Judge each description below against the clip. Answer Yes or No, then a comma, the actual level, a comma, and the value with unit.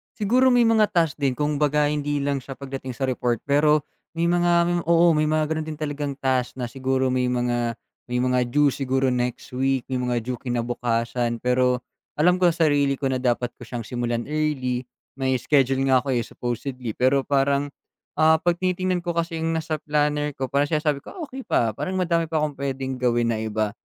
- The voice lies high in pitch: No, medium, 140 Hz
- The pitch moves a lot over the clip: No, average, 3.7 semitones